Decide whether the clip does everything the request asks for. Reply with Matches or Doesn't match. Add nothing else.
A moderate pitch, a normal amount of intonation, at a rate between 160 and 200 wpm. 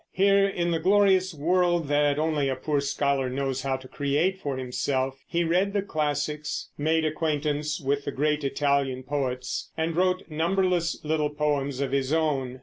Matches